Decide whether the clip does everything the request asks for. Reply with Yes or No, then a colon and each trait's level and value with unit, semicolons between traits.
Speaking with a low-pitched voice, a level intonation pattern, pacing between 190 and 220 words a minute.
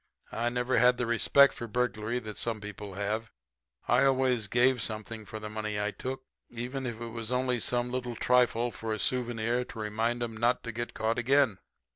Yes: low, 120 Hz; narrow, 2.2 semitones; average, 195 wpm